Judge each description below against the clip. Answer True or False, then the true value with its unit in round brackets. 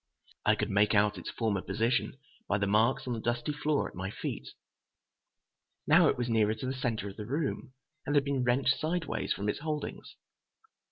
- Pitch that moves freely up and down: False (4.7 semitones)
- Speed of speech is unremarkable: True (190 wpm)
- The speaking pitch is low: True (120 Hz)